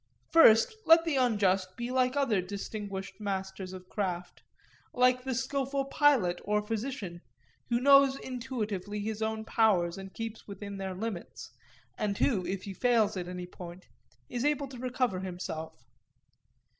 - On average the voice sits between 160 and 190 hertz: No, high, 210 Hz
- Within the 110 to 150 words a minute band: Yes, average, 145 wpm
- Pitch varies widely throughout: No, average, 5.0 semitones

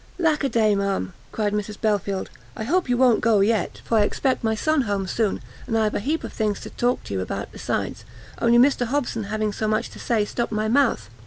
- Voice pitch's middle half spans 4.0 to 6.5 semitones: No, average, 3.0 semitones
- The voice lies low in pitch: No, high, 220 Hz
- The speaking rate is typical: No, fast, 230 wpm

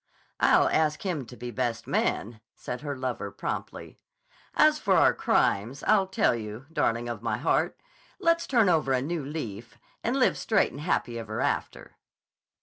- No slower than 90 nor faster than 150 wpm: No, average, 165 wpm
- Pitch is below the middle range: Yes, low, 130 Hz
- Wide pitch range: Yes, wide, 5.8 semitones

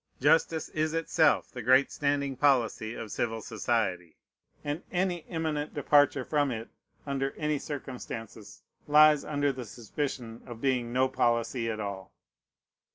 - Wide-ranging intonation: No, average, 4.2 semitones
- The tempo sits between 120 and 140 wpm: Yes, slow, 135 wpm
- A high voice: No, low, 135 Hz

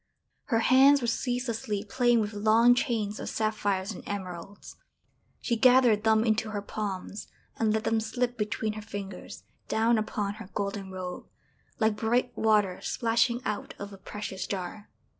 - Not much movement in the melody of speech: Yes, narrow, 2.3 semitones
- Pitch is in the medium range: No, high, 215 Hz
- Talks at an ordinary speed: Yes, average, 155 wpm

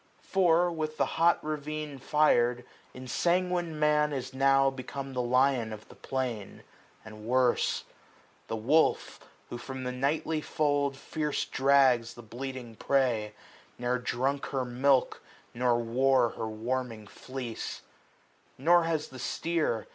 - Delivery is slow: Yes, slow, 130 wpm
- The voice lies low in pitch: Yes, low, 130 Hz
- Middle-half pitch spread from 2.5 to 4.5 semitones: Yes, average, 3.7 semitones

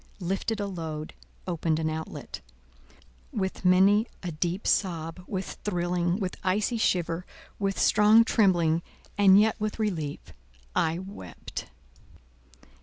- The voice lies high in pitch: No, medium, 180 Hz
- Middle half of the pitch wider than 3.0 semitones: Yes, average, 3.7 semitones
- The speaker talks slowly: Yes, slow, 110 wpm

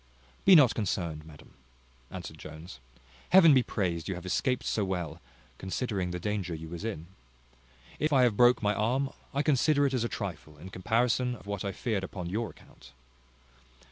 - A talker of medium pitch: No, low, 100 Hz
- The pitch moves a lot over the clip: Yes, wide, 6.1 semitones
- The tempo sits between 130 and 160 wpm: No, average, 175 wpm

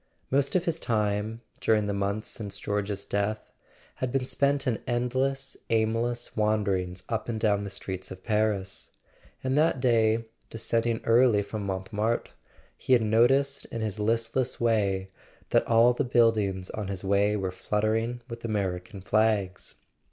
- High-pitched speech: No, low, 110 Hz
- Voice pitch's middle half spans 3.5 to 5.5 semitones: No, average, 2.8 semitones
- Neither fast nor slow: Yes, average, 150 wpm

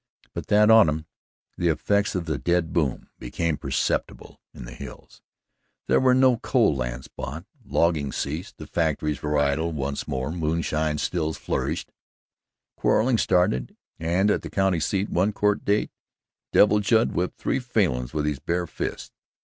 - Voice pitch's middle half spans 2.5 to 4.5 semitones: No, average, 5.2 semitones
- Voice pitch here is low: Yes, very low, 85 Hz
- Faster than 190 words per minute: No, average, 155 wpm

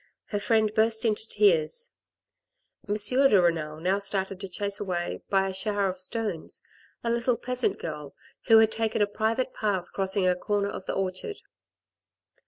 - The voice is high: Yes, high, 205 Hz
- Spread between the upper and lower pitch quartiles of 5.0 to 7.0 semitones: No, average, 3.0 semitones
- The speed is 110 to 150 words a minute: No, average, 165 wpm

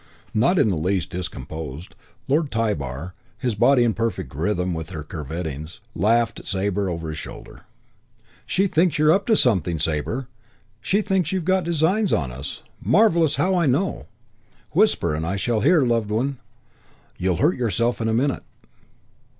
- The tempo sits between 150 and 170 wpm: Yes, average, 160 wpm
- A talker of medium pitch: No, low, 110 Hz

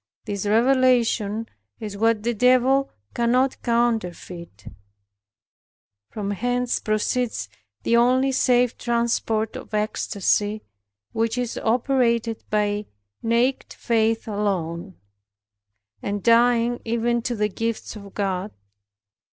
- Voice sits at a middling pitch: No, high, 230 Hz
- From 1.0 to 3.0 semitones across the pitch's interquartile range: Yes, narrow, 2.6 semitones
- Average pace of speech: No, slow, 100 wpm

